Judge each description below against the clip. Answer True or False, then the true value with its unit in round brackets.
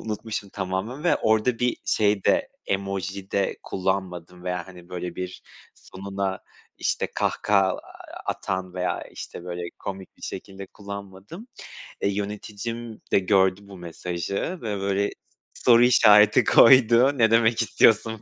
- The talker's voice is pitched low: True (100 Hz)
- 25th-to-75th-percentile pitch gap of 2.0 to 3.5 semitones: True (2.9 semitones)